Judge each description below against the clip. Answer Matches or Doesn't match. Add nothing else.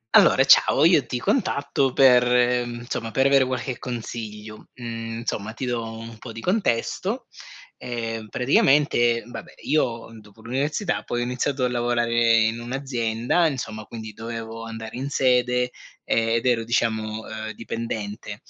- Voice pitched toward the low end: Matches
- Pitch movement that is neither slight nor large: Doesn't match